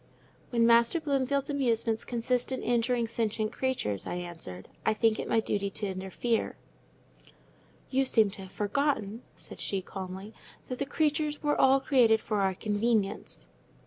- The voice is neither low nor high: No, high, 230 Hz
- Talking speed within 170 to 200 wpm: No, average, 150 wpm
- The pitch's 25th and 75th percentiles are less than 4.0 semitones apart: No, average, 4.5 semitones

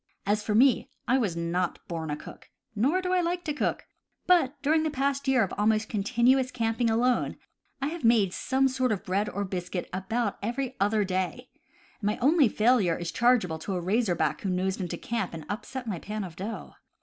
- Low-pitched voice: No, high, 220 Hz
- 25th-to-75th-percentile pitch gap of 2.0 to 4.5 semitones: No, wide, 5.5 semitones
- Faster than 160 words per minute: Yes, average, 200 wpm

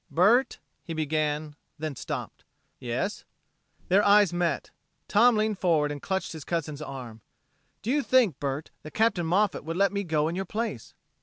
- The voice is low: No, medium, 170 Hz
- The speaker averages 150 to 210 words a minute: Yes, average, 165 wpm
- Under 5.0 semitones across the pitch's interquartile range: No, wide, 5.4 semitones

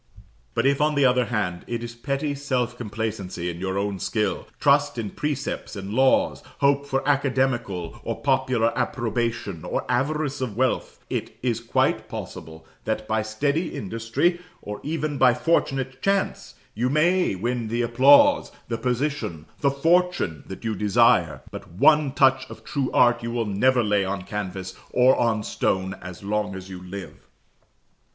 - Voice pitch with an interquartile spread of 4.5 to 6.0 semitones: Yes, average, 5.1 semitones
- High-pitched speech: No, low, 120 Hz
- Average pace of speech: Yes, average, 160 wpm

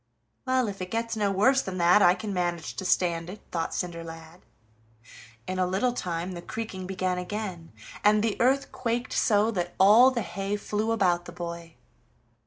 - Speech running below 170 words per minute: No, average, 180 wpm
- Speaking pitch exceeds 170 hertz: Yes, high, 190 Hz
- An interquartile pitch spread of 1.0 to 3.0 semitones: No, average, 3.7 semitones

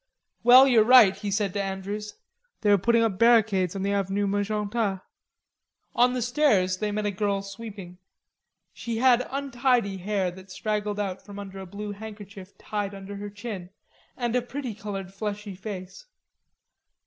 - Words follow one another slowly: No, average, 160 wpm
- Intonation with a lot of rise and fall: No, average, 2.7 semitones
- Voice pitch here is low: No, high, 205 Hz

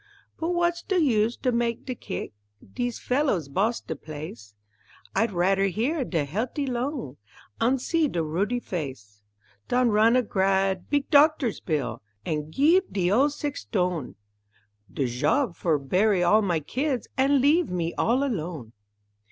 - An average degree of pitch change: No, wide, 8.3 semitones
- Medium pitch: No, high, 215 Hz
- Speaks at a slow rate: No, average, 150 wpm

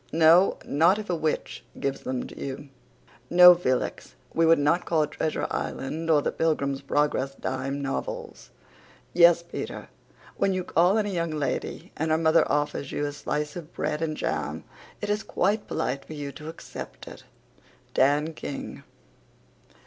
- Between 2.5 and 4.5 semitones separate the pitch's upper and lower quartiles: Yes, average, 3.2 semitones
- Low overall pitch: No, medium, 155 Hz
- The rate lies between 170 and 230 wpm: Yes, average, 175 wpm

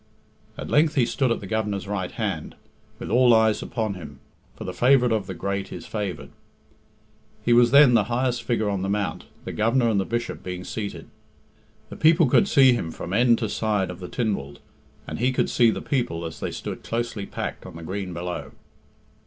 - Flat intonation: No, average, 4.2 semitones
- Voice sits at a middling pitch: No, low, 110 Hz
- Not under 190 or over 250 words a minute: Yes, average, 200 wpm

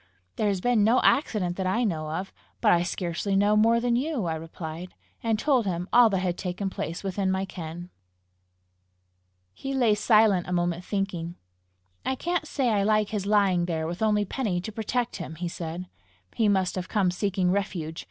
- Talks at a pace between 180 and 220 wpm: Yes, average, 190 wpm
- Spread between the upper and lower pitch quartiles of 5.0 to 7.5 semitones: No, average, 3.7 semitones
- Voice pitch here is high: Yes, high, 195 Hz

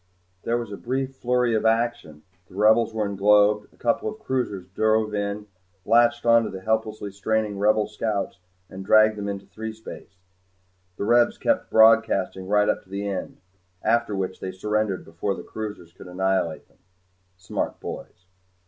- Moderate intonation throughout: No, narrow, 2.3 semitones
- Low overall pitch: Yes, low, 105 Hz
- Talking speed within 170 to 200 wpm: No, average, 160 wpm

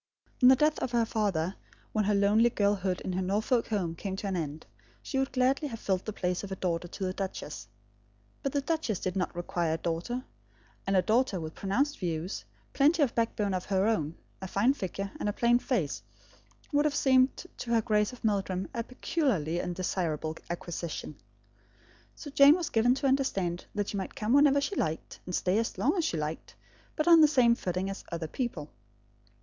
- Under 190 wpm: No, average, 200 wpm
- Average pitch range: No, wide, 5.9 semitones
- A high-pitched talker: Yes, high, 205 Hz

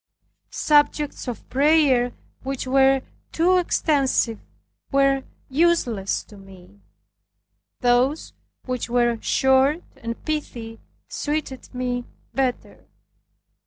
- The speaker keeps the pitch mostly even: No, average, 3.3 semitones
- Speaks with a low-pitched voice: No, very high, 265 Hz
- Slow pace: Yes, slow, 90 wpm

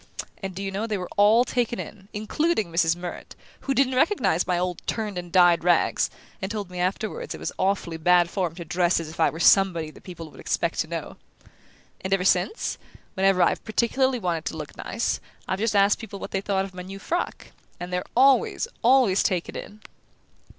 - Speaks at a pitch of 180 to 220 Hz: Yes, high, 190 Hz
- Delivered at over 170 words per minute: Yes, fast, 205 wpm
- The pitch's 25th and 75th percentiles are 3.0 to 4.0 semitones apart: Yes, average, 3.5 semitones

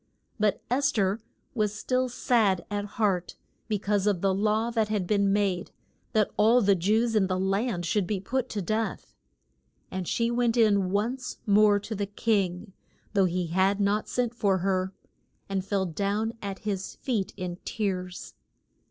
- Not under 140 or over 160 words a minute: No, average, 170 wpm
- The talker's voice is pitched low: No, high, 205 Hz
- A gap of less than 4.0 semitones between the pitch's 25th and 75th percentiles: Yes, narrow, 2.5 semitones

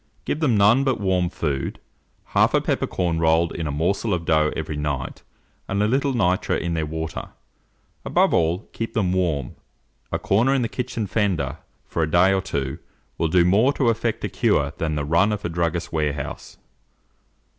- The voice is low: Yes, very low, 90 Hz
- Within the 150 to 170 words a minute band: No, average, 185 wpm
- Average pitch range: Yes, average, 5.0 semitones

